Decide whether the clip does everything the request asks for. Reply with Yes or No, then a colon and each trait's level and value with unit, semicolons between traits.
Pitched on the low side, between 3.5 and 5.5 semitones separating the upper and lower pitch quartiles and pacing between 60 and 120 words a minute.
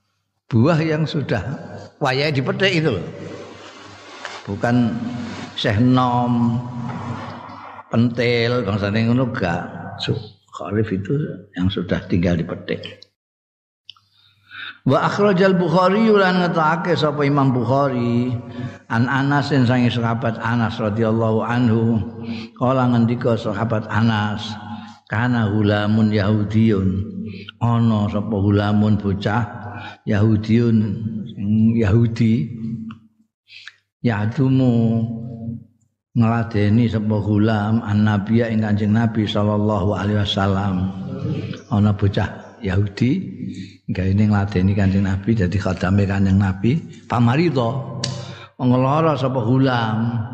No: low, 115 Hz; average, 2.8 semitones; slow, 85 wpm